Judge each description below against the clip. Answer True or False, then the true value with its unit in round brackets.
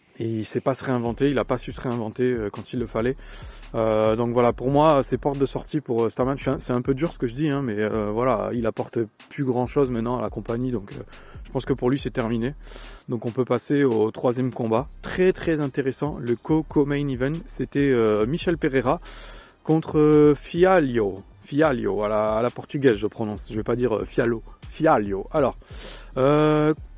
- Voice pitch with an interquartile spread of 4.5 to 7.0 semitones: False (3.6 semitones)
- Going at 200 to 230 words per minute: True (220 wpm)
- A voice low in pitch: True (130 Hz)